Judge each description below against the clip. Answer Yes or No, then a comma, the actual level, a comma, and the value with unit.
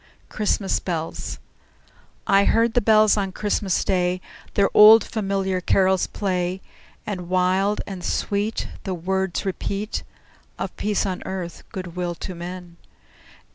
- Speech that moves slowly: Yes, slow, 130 wpm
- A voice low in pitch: No, high, 190 Hz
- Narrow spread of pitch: Yes, narrow, 2.1 semitones